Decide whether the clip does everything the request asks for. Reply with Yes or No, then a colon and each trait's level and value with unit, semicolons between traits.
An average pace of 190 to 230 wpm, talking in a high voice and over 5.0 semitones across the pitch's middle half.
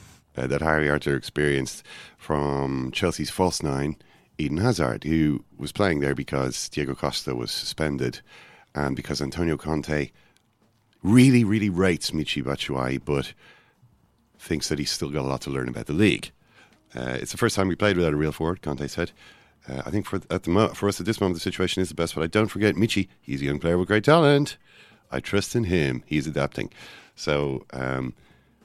No: average, 195 wpm; very low, 75 Hz; wide, 5.4 semitones